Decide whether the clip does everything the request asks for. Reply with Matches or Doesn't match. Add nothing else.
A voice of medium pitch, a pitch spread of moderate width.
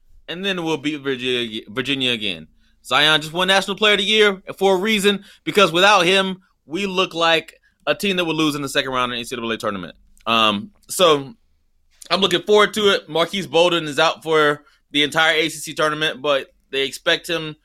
Doesn't match